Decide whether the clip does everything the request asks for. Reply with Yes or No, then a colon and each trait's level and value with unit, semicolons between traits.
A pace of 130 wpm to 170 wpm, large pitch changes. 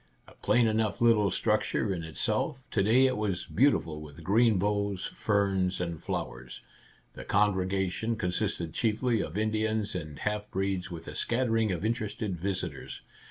No: average, 150 wpm; average, 3.3 semitones